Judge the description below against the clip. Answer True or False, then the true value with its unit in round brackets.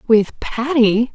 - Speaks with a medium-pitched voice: False (240 Hz)